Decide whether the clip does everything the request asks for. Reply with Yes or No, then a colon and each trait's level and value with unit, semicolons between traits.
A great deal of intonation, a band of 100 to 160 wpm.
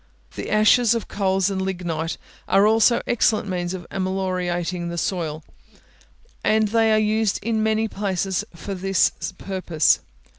No: average, 3.2 semitones; average, 140 wpm